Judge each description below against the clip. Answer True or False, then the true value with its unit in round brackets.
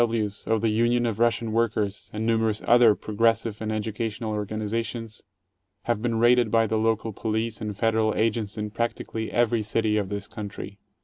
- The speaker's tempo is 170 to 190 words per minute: True (180 wpm)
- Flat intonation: True (1.4 semitones)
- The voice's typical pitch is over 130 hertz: False (110 Hz)